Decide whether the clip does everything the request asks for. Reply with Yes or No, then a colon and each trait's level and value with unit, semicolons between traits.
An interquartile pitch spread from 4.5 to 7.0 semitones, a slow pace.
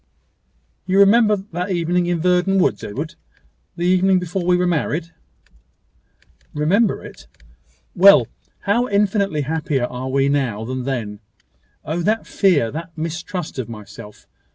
Yes: wide, 5.5 semitones; slow, 130 wpm